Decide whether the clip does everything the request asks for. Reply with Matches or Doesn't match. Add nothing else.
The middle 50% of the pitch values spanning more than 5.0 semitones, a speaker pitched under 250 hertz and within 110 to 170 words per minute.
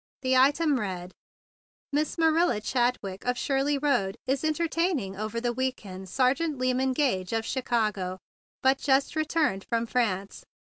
Doesn't match